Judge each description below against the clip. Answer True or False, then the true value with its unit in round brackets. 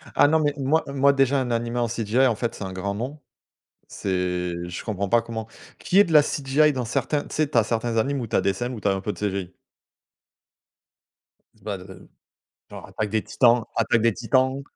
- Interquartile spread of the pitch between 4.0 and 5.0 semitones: True (4.6 semitones)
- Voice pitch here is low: True (115 Hz)